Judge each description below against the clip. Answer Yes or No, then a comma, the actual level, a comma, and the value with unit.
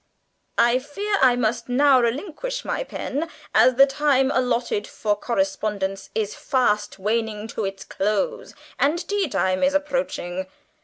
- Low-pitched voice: No, high, 245 Hz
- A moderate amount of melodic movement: No, wide, 5.7 semitones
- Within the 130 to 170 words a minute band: Yes, average, 140 wpm